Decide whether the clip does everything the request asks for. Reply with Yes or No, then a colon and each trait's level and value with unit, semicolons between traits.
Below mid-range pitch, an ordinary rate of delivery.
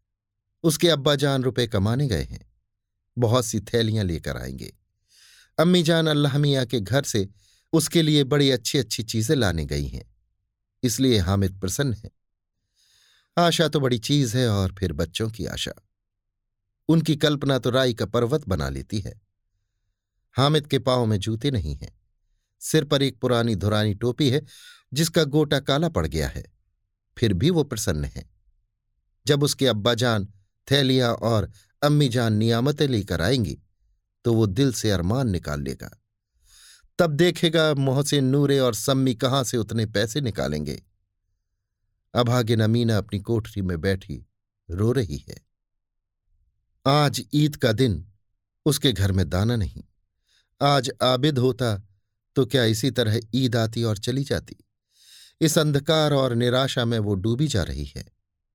Yes: low, 115 Hz; average, 145 wpm